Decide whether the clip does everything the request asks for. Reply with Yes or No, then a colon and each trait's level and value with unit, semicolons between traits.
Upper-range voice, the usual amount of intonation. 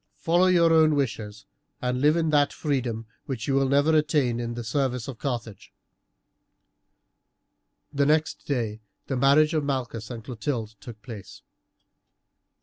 No: low, 135 Hz; average, 4.3 semitones